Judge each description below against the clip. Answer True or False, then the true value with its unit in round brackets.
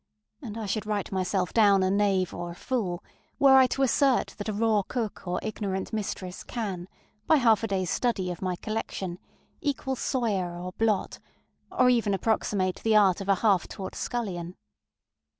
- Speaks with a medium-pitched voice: False (205 Hz)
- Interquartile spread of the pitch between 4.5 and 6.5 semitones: False (3.4 semitones)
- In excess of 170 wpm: True (180 wpm)